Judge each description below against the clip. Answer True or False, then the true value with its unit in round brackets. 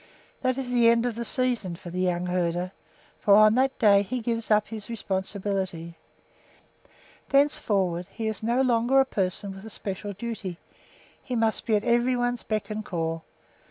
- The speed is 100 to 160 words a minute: False (175 wpm)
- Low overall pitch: False (215 Hz)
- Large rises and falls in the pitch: False (4.1 semitones)